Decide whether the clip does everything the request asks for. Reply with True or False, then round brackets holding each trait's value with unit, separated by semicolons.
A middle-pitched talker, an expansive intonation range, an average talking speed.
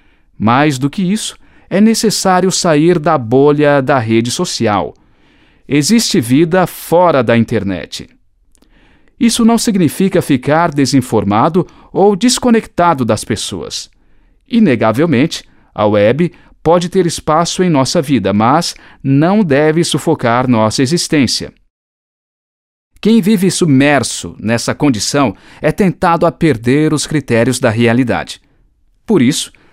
False (155 Hz; 6.1 semitones; 115 wpm)